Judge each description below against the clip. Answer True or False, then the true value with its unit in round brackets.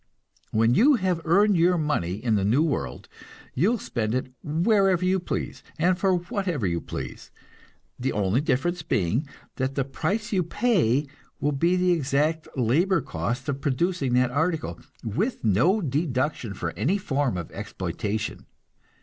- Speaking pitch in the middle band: True (150 Hz)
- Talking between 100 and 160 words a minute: True (155 wpm)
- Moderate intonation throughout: False (6.6 semitones)